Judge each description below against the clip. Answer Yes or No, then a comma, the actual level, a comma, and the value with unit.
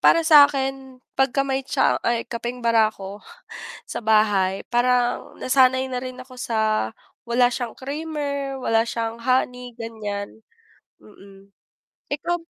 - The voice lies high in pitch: Yes, very high, 250 Hz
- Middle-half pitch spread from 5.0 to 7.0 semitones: No, average, 3.3 semitones